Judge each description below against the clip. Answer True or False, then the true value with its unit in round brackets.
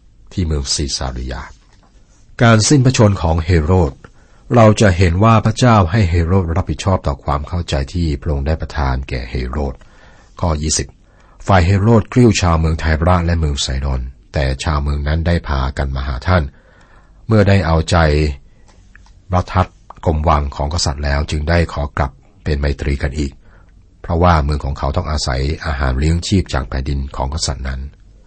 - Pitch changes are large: False (4.5 semitones)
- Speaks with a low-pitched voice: True (80 Hz)